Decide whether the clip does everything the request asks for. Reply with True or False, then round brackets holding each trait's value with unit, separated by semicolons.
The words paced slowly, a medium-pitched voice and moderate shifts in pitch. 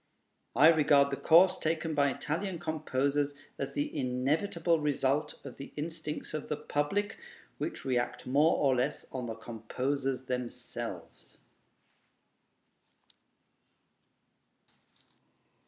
True (105 wpm; 145 Hz; 3.2 semitones)